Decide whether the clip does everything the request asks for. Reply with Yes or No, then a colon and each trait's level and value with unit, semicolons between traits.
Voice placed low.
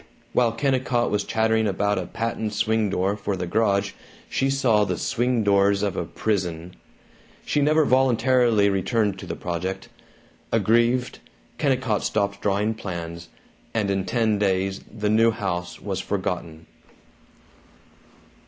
Yes: low, 105 Hz